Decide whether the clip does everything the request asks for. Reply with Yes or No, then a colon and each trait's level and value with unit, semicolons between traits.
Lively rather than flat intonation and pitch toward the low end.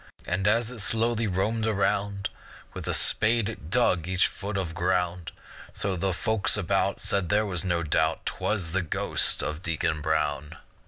No: average, 3.7 semitones; very low, 95 Hz